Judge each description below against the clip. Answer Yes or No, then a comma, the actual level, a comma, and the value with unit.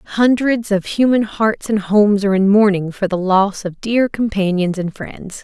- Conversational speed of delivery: Yes, average, 190 wpm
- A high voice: Yes, high, 205 Hz